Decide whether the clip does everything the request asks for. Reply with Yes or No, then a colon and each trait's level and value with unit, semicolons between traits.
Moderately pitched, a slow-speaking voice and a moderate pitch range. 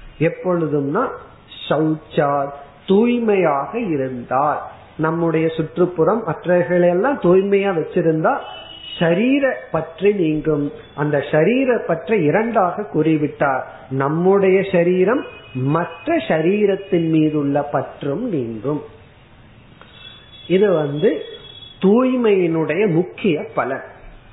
Yes: medium, 165 Hz; slow, 70 wpm; average, 4.5 semitones